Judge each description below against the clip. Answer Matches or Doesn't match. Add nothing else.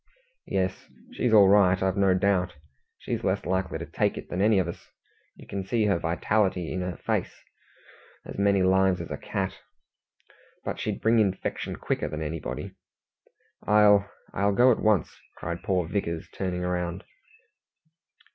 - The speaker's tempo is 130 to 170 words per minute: Matches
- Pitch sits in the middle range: Doesn't match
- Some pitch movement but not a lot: Doesn't match